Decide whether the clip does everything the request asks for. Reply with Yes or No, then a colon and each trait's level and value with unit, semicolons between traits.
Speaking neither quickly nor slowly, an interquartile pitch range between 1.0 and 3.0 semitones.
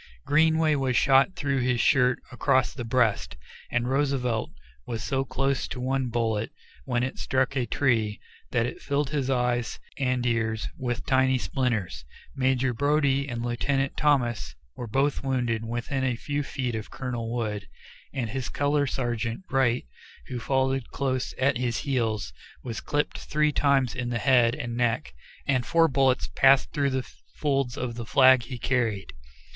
Yes: average, 160 wpm; narrow, 2.4 semitones